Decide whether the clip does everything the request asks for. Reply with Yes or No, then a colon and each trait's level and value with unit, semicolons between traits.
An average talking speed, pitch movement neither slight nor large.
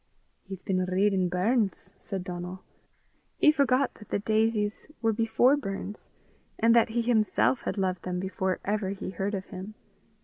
Yes: average, 160 wpm; average, 3.2 semitones